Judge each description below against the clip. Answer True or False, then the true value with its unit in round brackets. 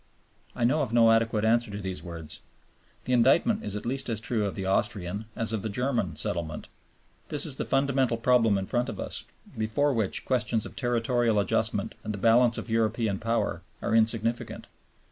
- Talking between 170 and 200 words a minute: True (185 wpm)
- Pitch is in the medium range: False (115 Hz)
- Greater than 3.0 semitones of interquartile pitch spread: False (2.7 semitones)